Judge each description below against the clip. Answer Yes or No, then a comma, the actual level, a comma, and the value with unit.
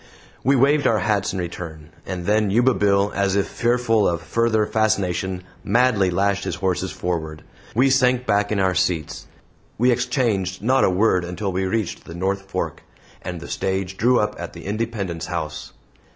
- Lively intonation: No, average, 3.9 semitones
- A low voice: Yes, low, 100 Hz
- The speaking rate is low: No, average, 180 wpm